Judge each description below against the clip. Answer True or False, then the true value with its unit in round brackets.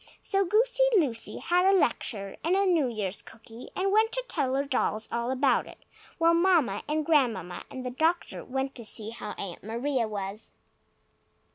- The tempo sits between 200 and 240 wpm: False (175 wpm)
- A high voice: True (265 Hz)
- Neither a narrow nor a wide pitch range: False (7.3 semitones)